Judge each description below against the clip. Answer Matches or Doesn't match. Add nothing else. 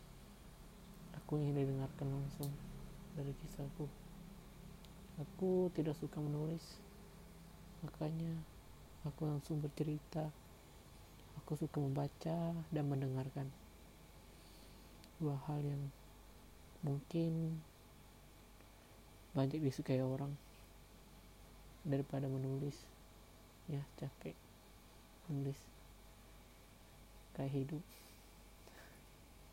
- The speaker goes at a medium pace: Doesn't match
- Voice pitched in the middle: Matches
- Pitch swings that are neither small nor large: Matches